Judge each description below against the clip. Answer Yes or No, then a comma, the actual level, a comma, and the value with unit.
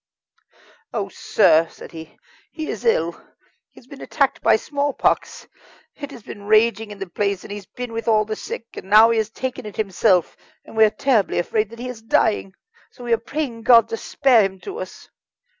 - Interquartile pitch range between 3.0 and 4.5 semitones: Yes, average, 3.4 semitones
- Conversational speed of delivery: No, fast, 210 wpm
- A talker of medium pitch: No, high, 225 Hz